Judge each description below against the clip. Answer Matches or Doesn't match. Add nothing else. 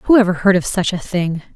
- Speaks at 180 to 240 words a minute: Doesn't match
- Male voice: Doesn't match